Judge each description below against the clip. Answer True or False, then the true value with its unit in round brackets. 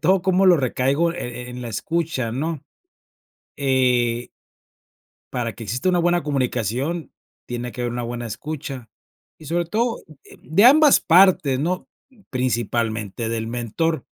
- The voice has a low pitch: True (130 Hz)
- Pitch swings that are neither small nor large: False (5.9 semitones)